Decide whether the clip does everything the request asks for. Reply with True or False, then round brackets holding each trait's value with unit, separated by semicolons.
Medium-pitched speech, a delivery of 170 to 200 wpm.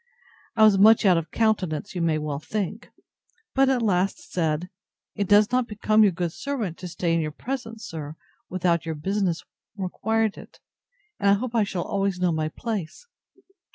False (195 Hz; 180 wpm)